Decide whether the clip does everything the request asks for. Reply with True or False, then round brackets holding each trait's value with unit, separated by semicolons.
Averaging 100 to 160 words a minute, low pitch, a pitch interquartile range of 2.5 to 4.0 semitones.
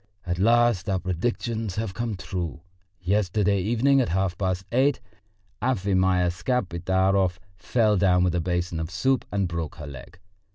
True (150 wpm; 95 Hz; 3.7 semitones)